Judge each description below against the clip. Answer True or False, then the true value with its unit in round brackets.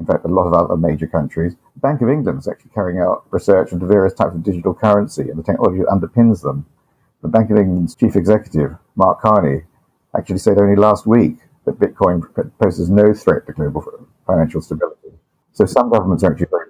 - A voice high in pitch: False (100 Hz)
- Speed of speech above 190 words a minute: True (200 wpm)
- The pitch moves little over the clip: False (4.1 semitones)